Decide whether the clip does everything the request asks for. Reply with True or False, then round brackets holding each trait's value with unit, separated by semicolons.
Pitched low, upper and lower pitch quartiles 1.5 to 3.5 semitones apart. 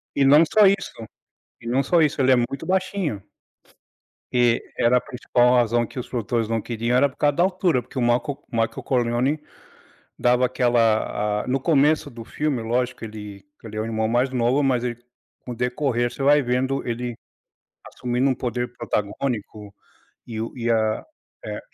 True (125 Hz; 2.8 semitones)